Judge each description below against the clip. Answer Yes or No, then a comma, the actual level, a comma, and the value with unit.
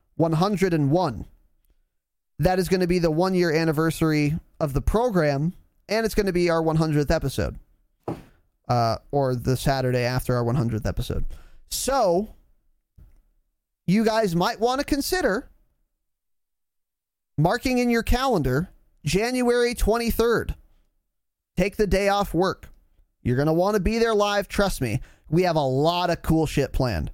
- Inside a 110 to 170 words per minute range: Yes, average, 145 wpm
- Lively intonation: Yes, wide, 7.8 semitones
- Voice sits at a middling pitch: Yes, medium, 165 Hz